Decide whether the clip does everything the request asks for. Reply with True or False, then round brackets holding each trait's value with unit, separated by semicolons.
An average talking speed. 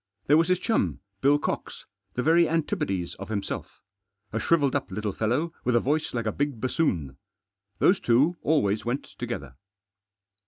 True (160 wpm)